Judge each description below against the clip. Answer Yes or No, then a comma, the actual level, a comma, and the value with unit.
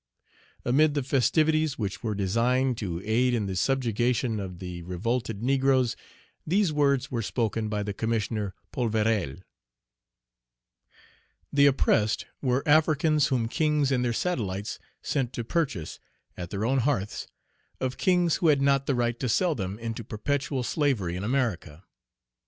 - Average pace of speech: Yes, average, 145 wpm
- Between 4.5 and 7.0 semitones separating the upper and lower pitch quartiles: Yes, average, 4.8 semitones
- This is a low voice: Yes, low, 120 Hz